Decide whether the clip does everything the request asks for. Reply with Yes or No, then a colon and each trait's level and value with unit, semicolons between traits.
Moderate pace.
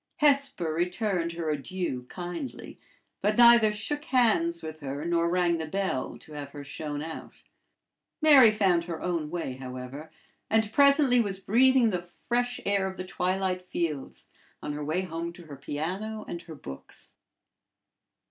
Yes: average, 155 wpm